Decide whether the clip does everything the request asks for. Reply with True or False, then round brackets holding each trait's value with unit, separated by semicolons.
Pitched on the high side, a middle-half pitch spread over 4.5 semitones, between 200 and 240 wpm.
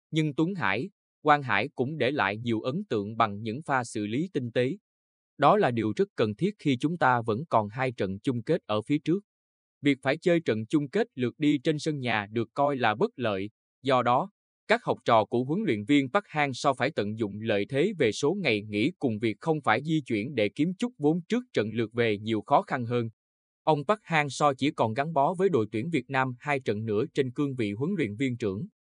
False (130 Hz; 5.5 semitones; 235 wpm)